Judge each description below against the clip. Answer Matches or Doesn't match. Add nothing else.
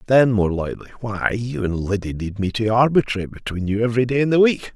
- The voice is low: Matches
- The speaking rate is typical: Doesn't match